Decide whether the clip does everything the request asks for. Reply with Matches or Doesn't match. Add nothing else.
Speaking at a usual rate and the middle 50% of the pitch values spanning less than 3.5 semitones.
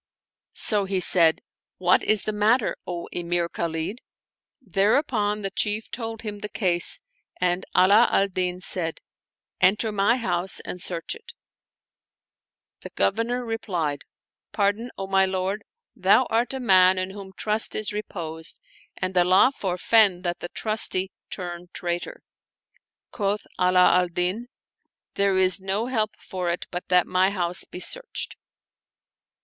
Matches